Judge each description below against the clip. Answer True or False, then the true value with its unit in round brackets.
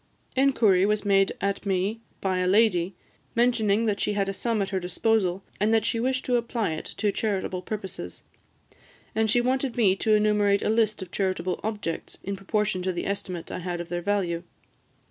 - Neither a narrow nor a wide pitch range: True (3.0 semitones)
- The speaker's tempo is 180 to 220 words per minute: True (190 wpm)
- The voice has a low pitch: False (200 Hz)